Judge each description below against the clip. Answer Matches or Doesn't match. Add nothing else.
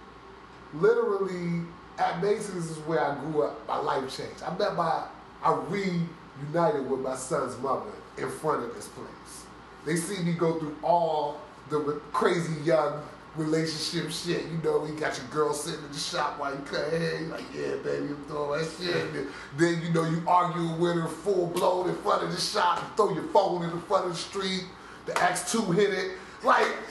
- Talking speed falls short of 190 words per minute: Doesn't match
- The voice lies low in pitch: Doesn't match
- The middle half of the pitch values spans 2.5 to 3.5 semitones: Matches